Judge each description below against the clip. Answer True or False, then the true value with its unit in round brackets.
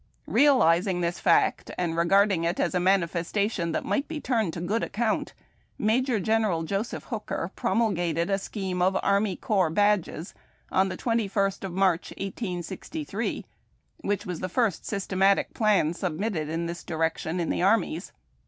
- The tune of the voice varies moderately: True (3.7 semitones)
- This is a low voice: False (190 Hz)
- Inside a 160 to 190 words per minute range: False (150 wpm)